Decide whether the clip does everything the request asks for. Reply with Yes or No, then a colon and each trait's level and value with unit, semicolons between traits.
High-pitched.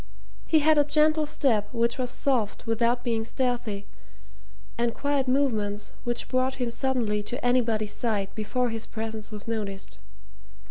Yes: high, 235 Hz